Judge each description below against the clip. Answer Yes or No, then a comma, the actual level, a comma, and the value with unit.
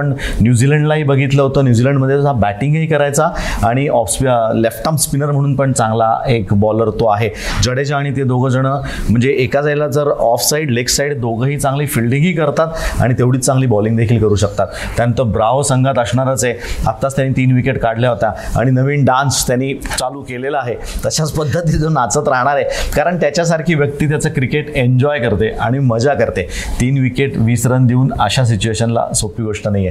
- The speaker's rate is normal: No, fast, 175 wpm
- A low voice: Yes, low, 130 Hz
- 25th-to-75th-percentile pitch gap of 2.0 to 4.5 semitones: Yes, average, 3.6 semitones